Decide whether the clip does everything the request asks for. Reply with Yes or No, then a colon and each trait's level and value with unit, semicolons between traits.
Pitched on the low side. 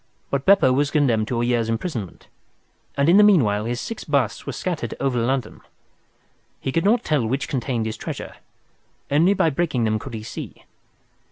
Yes: low, 130 Hz